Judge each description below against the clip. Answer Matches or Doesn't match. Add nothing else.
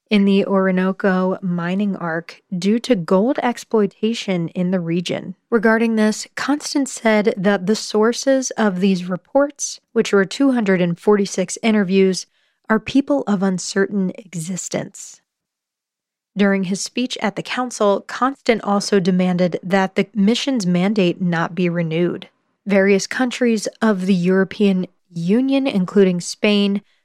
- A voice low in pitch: Doesn't match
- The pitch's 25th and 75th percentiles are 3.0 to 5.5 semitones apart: Matches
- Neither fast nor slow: Doesn't match